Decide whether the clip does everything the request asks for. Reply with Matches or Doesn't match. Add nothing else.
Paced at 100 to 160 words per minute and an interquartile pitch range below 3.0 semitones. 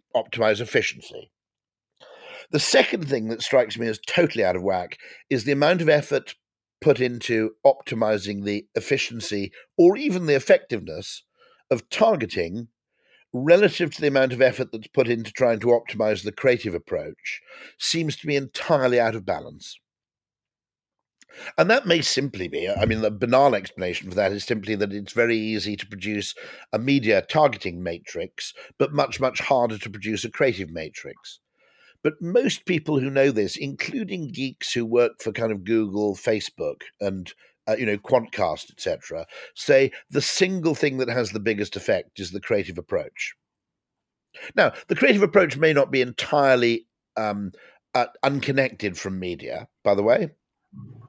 Doesn't match